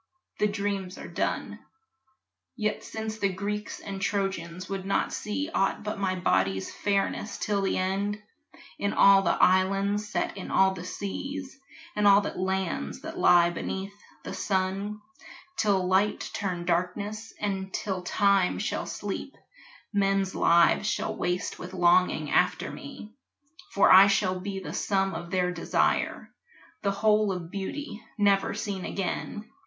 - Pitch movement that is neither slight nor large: No, narrow, 1.8 semitones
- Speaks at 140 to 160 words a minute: Yes, average, 145 wpm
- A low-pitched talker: No, high, 195 Hz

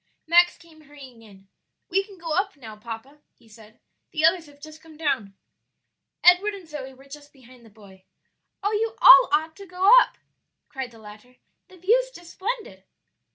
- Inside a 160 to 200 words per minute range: Yes, average, 175 wpm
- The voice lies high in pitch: Yes, very high, 300 Hz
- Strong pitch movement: Yes, wide, 7.5 semitones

